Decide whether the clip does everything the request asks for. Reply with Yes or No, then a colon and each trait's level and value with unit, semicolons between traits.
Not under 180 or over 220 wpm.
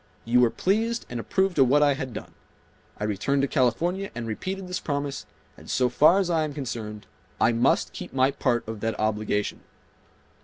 Yes: average, 190 wpm